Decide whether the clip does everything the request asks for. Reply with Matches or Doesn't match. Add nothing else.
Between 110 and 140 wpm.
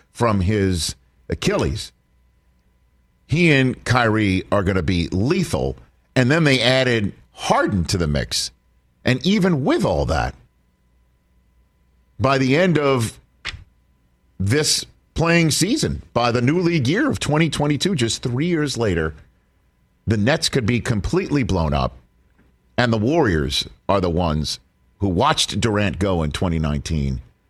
Matches